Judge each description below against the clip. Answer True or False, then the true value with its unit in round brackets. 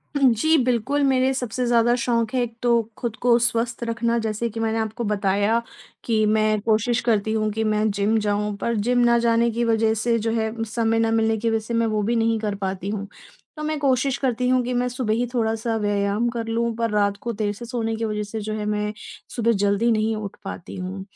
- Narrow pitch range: True (1.9 semitones)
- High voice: True (225 Hz)